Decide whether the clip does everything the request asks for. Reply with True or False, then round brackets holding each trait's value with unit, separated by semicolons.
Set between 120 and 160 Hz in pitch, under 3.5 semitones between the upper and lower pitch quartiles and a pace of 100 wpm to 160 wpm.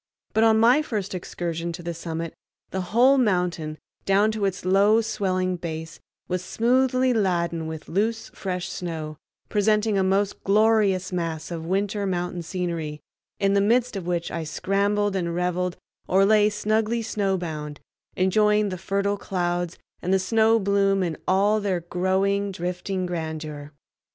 False (190 Hz; 3.1 semitones; 150 wpm)